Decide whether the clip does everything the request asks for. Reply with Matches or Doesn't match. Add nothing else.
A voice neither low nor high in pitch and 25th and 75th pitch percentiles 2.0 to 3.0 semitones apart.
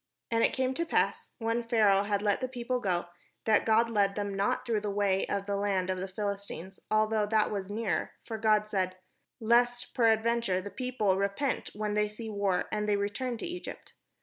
Doesn't match